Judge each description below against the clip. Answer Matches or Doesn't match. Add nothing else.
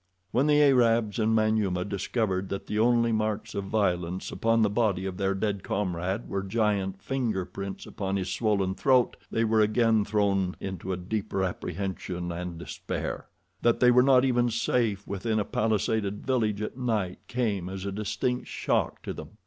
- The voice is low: Matches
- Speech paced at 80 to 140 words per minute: Doesn't match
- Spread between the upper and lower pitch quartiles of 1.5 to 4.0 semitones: Matches